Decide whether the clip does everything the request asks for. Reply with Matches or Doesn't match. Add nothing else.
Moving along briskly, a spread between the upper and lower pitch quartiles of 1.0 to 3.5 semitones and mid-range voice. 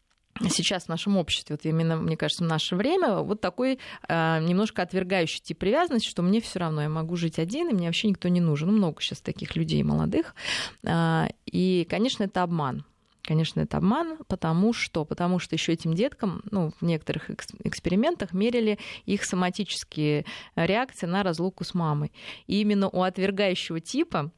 Doesn't match